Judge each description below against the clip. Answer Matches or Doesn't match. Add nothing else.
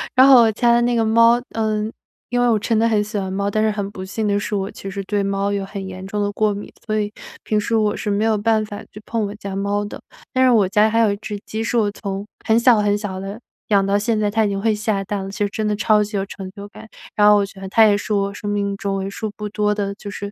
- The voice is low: Doesn't match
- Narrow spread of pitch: Matches